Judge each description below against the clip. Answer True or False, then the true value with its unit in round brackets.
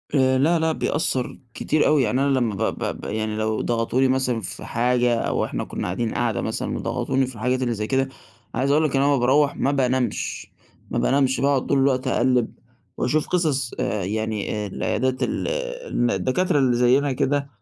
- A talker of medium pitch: False (130 Hz)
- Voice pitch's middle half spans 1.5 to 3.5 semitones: True (2.7 semitones)